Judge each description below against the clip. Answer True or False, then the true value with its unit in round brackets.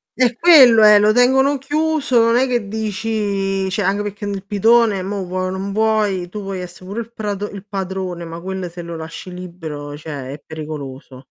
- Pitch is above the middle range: True (195 Hz)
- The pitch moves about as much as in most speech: True (3.7 semitones)